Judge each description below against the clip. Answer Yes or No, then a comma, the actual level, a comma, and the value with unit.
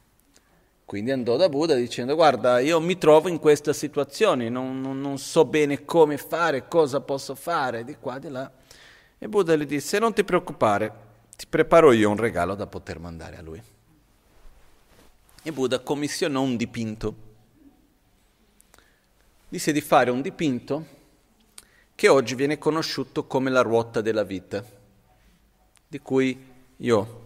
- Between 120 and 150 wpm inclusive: Yes, average, 145 wpm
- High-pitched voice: No, low, 135 Hz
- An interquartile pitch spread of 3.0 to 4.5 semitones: No, average, 5.0 semitones